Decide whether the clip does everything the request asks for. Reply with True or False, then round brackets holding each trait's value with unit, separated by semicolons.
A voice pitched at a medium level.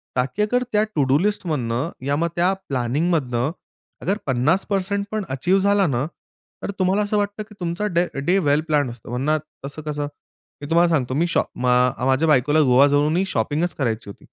True (150 Hz)